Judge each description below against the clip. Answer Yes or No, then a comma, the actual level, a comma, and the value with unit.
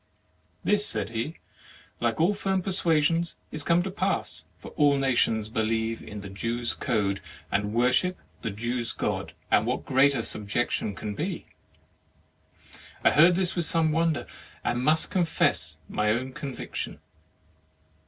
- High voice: No, low, 130 Hz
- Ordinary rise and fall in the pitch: No, wide, 6.9 semitones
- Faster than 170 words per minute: No, average, 140 wpm